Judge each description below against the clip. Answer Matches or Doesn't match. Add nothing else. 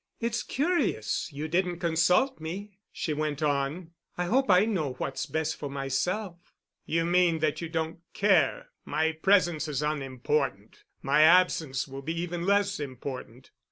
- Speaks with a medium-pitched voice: Matches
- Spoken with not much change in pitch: Doesn't match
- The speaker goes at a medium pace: Matches